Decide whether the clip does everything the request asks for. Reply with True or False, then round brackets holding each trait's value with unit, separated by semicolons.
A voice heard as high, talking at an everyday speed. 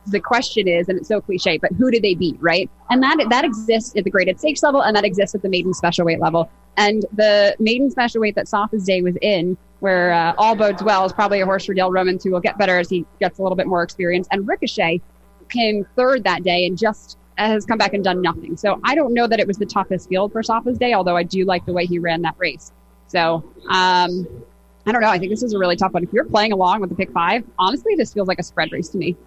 False (195 Hz; 270 wpm)